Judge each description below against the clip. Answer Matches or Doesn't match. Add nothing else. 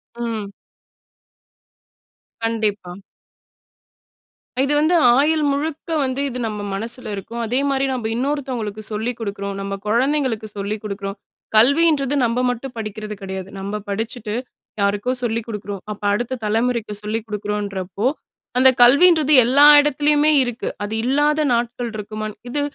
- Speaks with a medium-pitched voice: Doesn't match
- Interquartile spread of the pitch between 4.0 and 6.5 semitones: Matches